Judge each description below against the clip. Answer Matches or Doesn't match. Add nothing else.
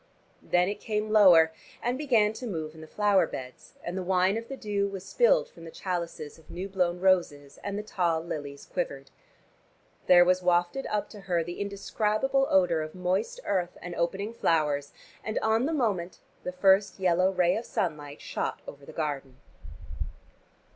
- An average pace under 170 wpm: Doesn't match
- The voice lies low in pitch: Doesn't match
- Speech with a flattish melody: Doesn't match